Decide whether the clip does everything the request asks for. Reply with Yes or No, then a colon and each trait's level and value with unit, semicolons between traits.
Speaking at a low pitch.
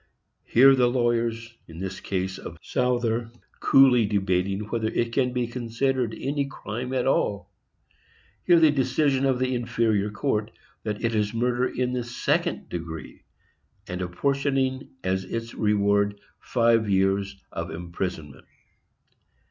Yes: low, 115 Hz